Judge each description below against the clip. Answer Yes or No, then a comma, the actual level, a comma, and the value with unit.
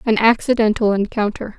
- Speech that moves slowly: Yes, slow, 115 wpm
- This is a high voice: Yes, high, 220 Hz